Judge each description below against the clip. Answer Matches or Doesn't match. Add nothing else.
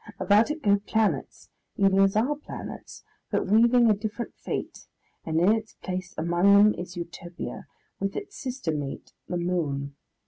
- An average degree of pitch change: Matches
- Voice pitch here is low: Doesn't match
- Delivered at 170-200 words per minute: Doesn't match